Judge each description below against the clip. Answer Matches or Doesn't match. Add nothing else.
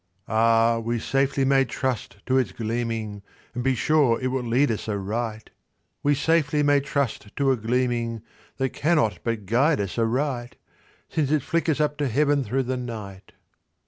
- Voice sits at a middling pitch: Doesn't match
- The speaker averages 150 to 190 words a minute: Matches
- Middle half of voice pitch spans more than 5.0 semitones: Doesn't match